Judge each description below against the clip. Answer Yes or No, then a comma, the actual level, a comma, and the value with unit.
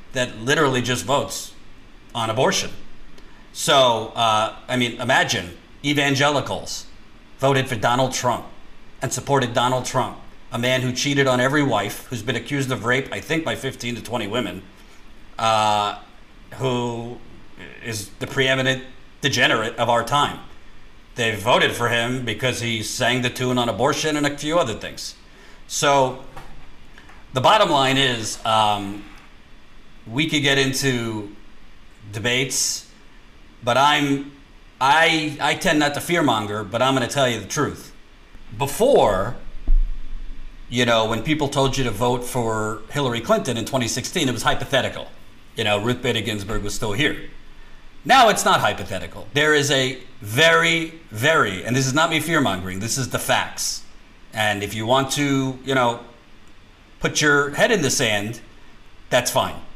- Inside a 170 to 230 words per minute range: No, average, 150 wpm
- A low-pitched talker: Yes, low, 125 Hz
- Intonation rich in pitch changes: No, average, 4.2 semitones